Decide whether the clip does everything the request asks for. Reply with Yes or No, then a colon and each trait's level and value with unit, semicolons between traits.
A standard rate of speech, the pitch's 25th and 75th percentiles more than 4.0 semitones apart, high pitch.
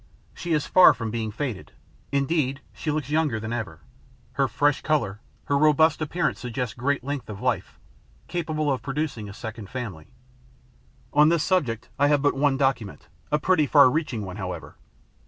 No: average, 170 wpm; average, 5.1 semitones; medium, 140 Hz